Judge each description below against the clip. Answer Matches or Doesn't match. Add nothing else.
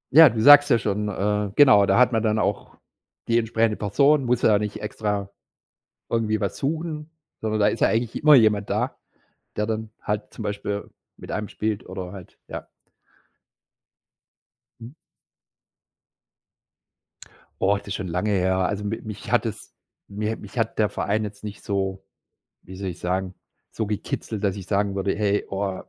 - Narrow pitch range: Matches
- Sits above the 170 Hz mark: Doesn't match